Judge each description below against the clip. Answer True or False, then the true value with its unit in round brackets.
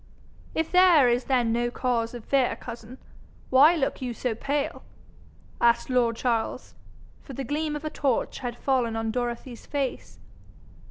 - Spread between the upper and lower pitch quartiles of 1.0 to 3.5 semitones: True (2.8 semitones)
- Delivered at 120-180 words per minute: True (155 wpm)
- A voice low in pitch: False (250 Hz)